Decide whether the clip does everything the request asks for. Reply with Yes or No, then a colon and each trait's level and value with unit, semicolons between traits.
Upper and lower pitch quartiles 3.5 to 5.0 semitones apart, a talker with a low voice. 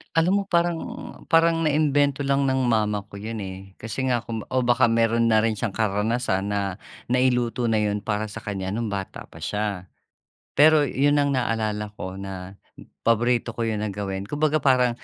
Yes: average, 4.3 semitones; low, 115 Hz